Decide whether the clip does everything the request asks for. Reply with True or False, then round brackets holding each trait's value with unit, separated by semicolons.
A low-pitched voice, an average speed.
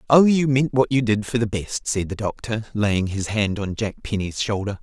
False (110 Hz; 235 wpm)